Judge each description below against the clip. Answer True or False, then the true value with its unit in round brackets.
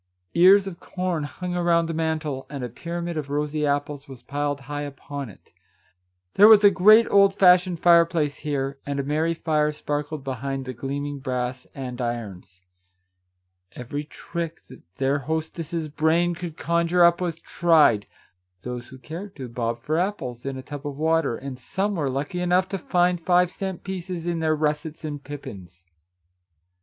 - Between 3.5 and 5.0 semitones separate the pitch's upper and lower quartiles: True (4.0 semitones)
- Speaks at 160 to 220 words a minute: True (165 wpm)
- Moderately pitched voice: True (150 Hz)